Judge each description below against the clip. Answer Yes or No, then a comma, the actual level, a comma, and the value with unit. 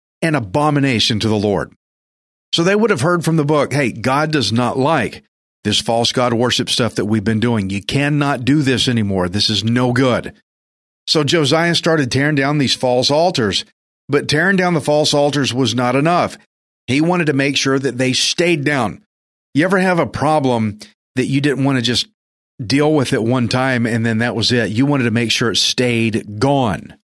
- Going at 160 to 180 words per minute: No, average, 200 wpm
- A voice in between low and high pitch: No, low, 130 Hz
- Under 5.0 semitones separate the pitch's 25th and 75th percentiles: Yes, average, 4.2 semitones